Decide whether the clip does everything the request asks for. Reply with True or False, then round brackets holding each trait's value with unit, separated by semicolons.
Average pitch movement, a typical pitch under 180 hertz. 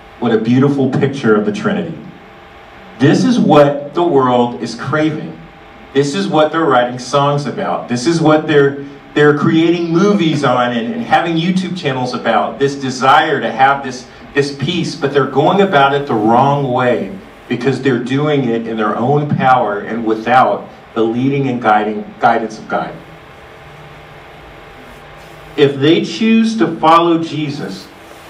True (4.1 semitones; 140 Hz)